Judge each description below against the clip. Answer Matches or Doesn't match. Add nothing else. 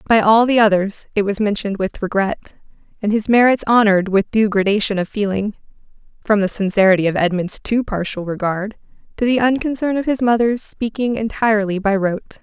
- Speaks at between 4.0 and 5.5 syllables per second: Doesn't match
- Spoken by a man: Doesn't match